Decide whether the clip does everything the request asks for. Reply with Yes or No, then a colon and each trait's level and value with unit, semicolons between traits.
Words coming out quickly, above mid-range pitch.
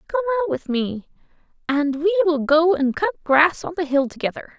No: average, 195 wpm; very high, 275 Hz